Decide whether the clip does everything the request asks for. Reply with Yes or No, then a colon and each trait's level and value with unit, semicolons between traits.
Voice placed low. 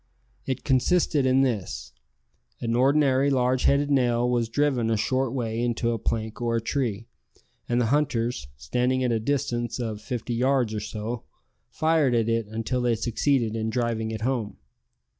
Yes: low, 120 Hz